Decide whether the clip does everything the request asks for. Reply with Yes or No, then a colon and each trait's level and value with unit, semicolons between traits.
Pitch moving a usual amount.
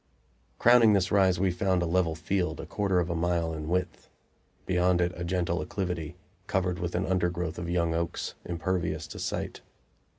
No: narrow, 1.5 semitones